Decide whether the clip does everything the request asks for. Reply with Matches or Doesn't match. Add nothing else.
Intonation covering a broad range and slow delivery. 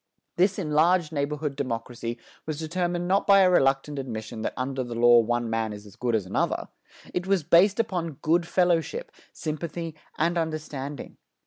Doesn't match